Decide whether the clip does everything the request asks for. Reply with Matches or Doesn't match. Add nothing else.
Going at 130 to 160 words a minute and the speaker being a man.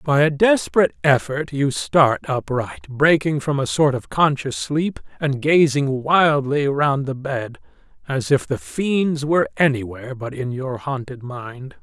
Matches